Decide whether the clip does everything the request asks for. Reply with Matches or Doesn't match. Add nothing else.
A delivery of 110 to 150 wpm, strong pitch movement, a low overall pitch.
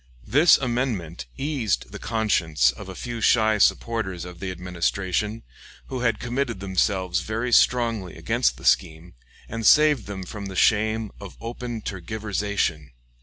Doesn't match